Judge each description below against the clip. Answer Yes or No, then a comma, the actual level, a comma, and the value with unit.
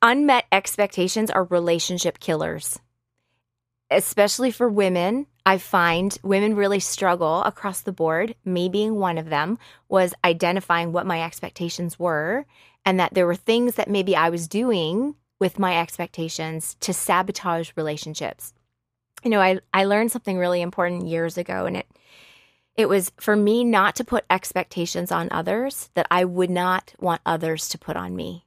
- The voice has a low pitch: No, medium, 180 Hz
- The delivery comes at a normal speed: Yes, average, 160 wpm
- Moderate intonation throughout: Yes, average, 3.3 semitones